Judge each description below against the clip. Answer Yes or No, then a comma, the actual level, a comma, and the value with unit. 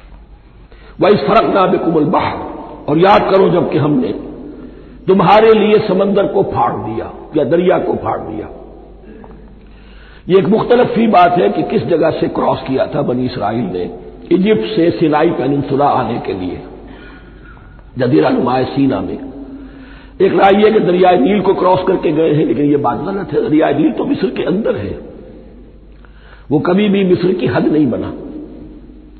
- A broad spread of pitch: Yes, wide, 5.8 semitones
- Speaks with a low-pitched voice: No, medium, 180 Hz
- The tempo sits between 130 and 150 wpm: No, average, 165 wpm